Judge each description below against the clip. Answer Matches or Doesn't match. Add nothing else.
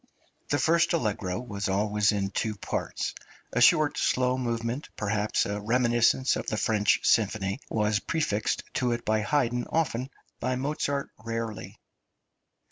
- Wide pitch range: Doesn't match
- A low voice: Matches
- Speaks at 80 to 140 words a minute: Matches